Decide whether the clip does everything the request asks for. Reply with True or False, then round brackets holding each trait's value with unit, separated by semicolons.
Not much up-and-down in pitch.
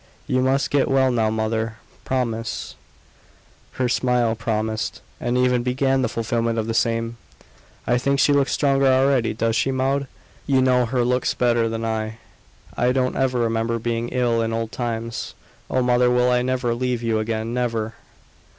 True (2.1 semitones)